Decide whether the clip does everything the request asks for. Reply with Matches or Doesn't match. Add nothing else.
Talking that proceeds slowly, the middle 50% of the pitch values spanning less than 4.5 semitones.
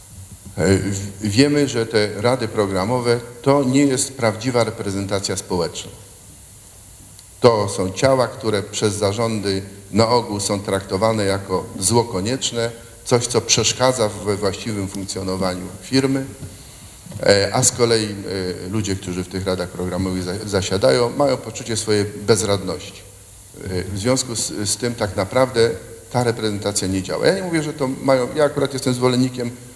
Doesn't match